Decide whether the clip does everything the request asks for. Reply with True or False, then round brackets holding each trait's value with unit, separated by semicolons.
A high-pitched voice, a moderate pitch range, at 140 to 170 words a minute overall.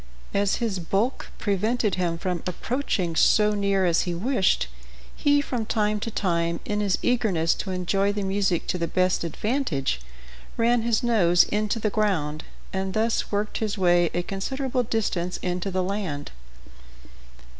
True (195 Hz; 3.7 semitones; 155 wpm)